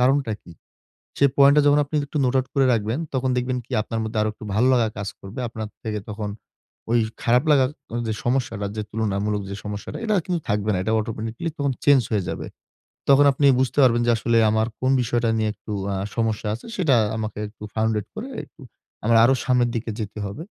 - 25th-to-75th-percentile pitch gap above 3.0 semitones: Yes, average, 3.4 semitones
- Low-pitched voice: Yes, low, 115 Hz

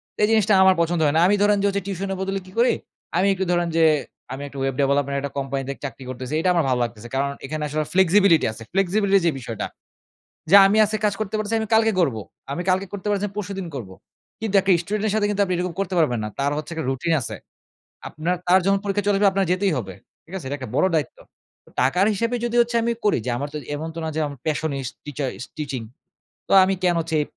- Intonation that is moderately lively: No, wide, 6.0 semitones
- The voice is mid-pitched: Yes, medium, 175 Hz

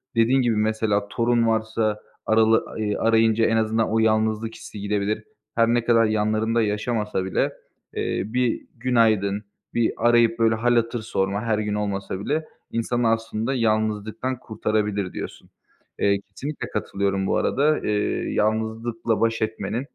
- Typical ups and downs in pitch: No, narrow, 1.6 semitones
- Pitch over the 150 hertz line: No, low, 110 Hz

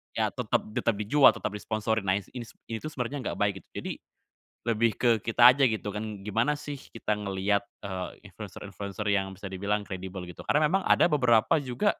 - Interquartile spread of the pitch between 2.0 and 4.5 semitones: Yes, average, 3.7 semitones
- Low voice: Yes, low, 110 Hz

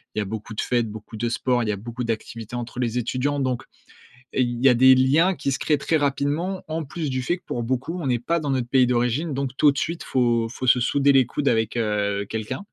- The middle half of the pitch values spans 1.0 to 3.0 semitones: No, average, 3.4 semitones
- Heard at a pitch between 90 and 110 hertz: No, low, 125 Hz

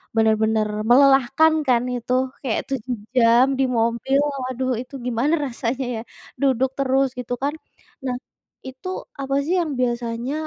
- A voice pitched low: No, very high, 255 Hz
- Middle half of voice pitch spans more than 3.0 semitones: No, narrow, 2.4 semitones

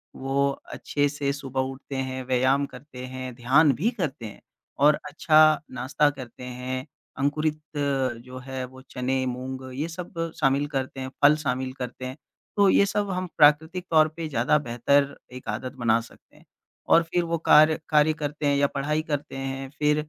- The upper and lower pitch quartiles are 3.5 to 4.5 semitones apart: No, average, 2.9 semitones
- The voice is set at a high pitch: No, medium, 140 Hz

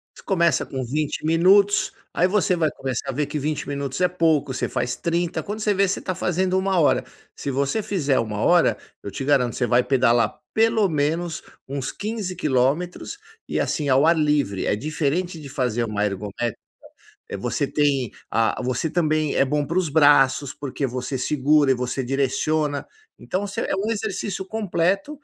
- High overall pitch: No, medium, 150 Hz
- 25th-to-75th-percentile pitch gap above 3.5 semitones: Yes, wide, 5.4 semitones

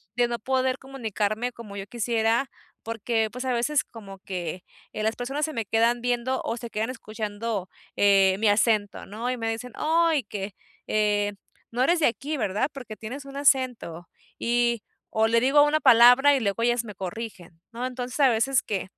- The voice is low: No, high, 230 Hz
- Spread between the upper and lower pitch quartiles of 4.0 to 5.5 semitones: No, average, 3.3 semitones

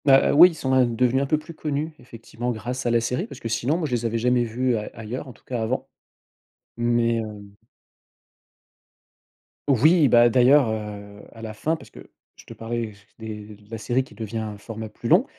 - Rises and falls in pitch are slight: No, average, 3.0 semitones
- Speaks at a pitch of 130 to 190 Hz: No, low, 120 Hz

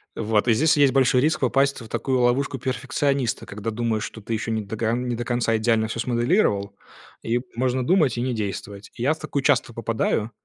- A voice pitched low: Yes, low, 120 Hz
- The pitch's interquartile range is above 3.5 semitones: No, average, 3.0 semitones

